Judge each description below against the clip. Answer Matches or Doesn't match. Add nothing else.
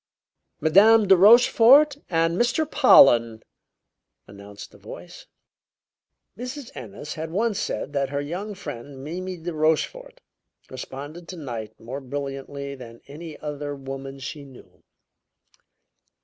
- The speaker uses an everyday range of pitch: Doesn't match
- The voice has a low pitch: Doesn't match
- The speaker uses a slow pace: Matches